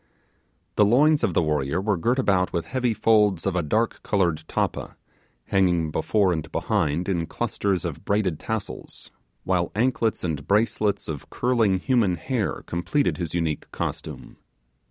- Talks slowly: No, average, 150 wpm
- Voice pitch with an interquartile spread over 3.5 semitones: Yes, average, 4.7 semitones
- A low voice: Yes, very low, 95 Hz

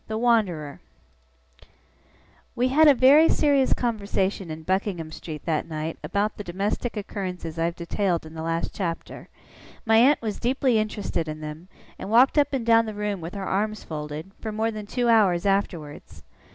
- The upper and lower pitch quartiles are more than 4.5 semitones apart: Yes, wide, 5.4 semitones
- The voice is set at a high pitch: Yes, high, 200 Hz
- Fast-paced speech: No, average, 175 wpm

